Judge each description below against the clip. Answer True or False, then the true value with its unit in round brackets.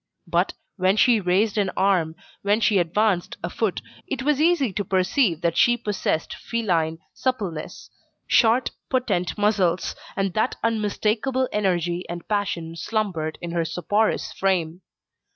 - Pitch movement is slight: False (4.2 semitones)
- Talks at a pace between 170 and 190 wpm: False (135 wpm)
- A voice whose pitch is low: False (200 Hz)